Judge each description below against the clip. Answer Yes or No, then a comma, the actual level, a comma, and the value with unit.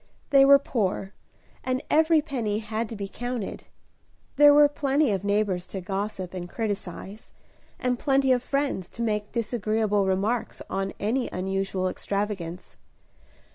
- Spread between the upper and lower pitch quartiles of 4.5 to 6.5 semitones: Yes, average, 4.8 semitones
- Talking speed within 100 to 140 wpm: Yes, slow, 135 wpm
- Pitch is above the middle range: Yes, high, 215 Hz